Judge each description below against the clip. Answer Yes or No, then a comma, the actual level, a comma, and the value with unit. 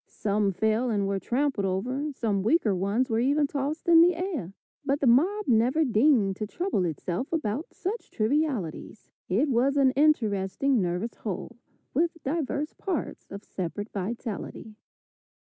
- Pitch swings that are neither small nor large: No, wide, 6.5 semitones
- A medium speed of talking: Yes, average, 145 wpm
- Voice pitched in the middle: No, high, 240 Hz